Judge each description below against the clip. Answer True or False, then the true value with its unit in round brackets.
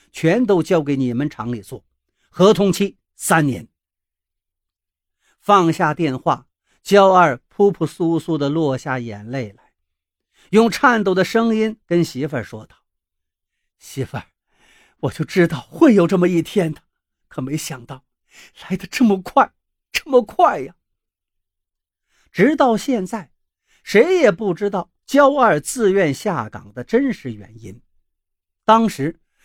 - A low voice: False (160 Hz)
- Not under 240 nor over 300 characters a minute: False (185 characters per minute)